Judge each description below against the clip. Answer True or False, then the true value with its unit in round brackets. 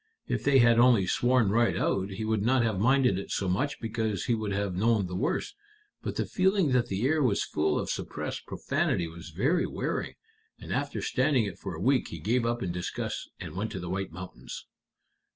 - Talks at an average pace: False (210 wpm)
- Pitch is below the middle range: True (110 Hz)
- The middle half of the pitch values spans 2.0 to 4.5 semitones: False (4.9 semitones)